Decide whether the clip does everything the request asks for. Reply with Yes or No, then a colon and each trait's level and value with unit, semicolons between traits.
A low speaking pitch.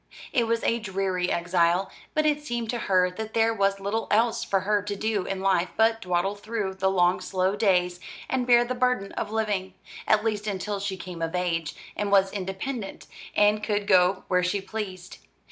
No: high, 200 Hz